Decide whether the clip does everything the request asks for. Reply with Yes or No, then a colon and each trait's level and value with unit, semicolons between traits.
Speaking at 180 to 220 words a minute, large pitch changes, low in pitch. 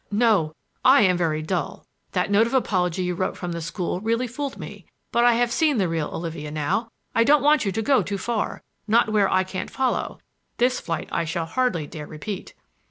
No: average, 200 wpm; wide, 5.8 semitones; high, 195 Hz